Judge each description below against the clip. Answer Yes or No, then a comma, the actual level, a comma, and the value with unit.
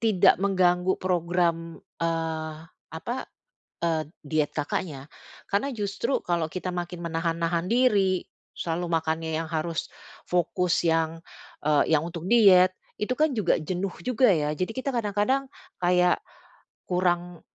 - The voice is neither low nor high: Yes, medium, 175 Hz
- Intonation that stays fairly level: No, average, 3.1 semitones